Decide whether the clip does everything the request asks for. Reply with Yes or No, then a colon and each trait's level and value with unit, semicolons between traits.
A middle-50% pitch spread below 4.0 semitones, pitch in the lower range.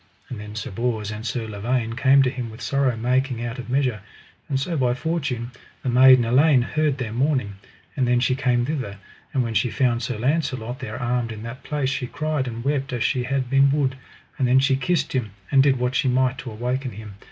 Yes: narrow, 2.4 semitones; low, 125 Hz